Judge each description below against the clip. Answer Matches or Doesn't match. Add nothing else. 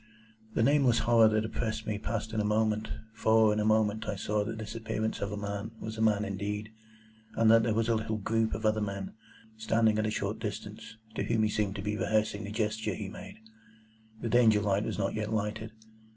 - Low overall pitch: Matches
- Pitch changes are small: Matches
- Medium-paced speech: Doesn't match